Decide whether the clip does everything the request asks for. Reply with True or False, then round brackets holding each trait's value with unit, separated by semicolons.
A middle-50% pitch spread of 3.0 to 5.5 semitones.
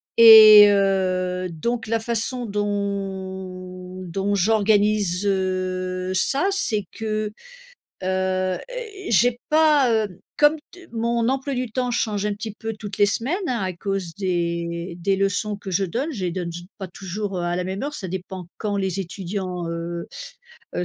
True (3.3 semitones)